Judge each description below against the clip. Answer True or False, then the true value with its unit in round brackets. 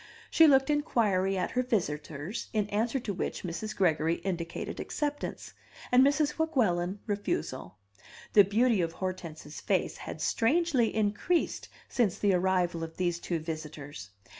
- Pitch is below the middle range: False (195 Hz)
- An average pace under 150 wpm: True (140 wpm)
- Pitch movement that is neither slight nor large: False (6.3 semitones)